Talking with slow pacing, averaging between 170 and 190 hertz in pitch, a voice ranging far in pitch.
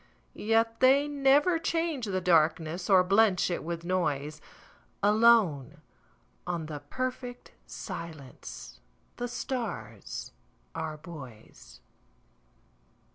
Yes: slow, 80 wpm; medium, 185 Hz; wide, 7.8 semitones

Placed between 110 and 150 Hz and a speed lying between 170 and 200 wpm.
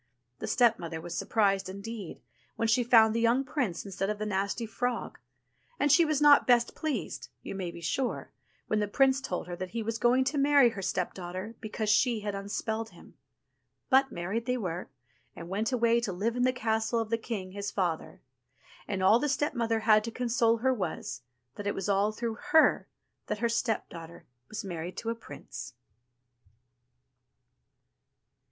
No: high, 220 Hz; average, 180 wpm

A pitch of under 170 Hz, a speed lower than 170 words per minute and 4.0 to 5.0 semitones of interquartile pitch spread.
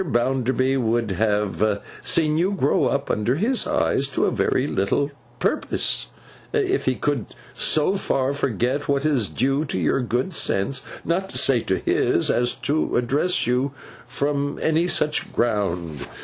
Yes: low, 135 Hz; average, 150 wpm; average, 4.4 semitones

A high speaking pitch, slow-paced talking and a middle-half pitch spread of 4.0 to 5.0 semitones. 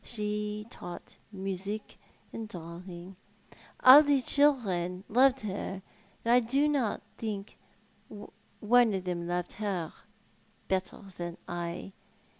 Yes: high, 205 Hz; slow, 105 wpm; average, 4.5 semitones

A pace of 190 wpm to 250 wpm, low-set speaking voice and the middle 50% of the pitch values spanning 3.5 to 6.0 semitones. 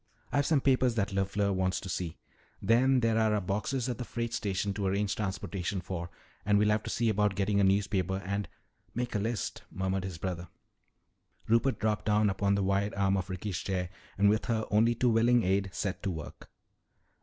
No: average, 200 wpm; low, 100 Hz; average, 2.7 semitones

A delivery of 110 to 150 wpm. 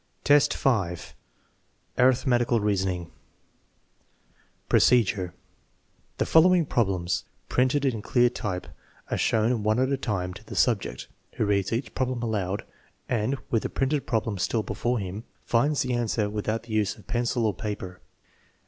Yes: average, 140 wpm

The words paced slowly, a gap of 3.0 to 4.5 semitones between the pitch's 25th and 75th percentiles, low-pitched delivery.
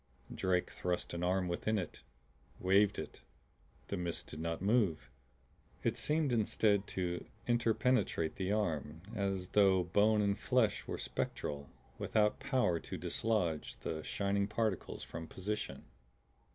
Yes: slow, 130 wpm; average, 3.6 semitones; low, 100 Hz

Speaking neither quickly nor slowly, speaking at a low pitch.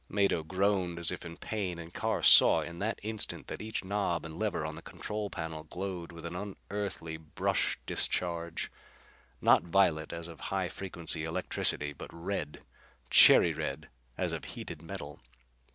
Yes: average, 160 wpm; very low, 85 Hz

